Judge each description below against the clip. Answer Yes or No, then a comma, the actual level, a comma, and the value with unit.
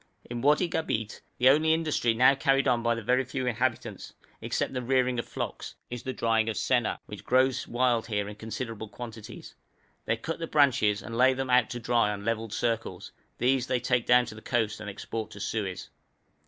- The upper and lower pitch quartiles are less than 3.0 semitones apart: Yes, narrow, 2.5 semitones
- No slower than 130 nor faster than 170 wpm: No, average, 200 wpm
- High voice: No, low, 120 Hz